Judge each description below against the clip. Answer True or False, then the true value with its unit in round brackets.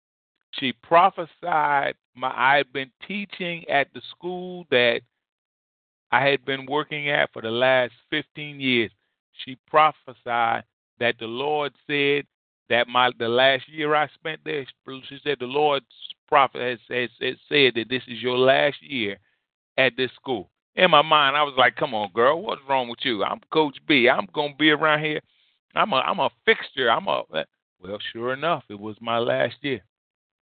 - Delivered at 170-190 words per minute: True (175 wpm)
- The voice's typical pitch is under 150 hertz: True (135 Hz)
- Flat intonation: False (3.8 semitones)